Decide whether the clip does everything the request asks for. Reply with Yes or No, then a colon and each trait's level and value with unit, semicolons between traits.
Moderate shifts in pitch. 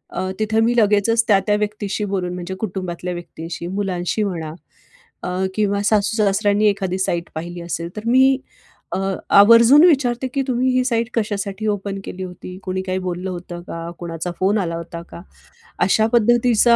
Yes: average, 3.7 semitones